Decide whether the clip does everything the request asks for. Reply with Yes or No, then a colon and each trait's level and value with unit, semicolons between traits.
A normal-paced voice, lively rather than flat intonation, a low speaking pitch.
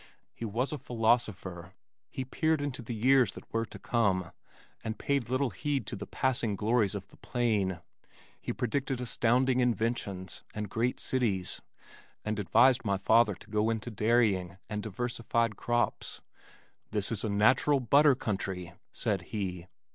No: average, 150 wpm; average, 3.5 semitones; low, 115 Hz